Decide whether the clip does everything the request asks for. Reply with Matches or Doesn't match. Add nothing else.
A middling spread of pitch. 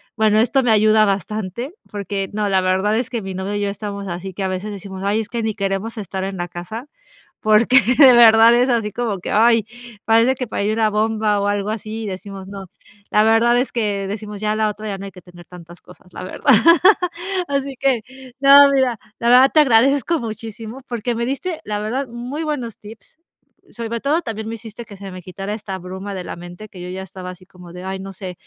Matches